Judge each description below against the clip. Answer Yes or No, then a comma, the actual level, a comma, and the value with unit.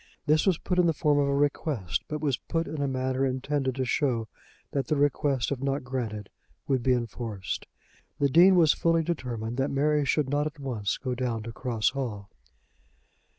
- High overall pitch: No, low, 135 Hz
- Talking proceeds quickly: No, average, 195 wpm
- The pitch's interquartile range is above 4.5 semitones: No, average, 3.2 semitones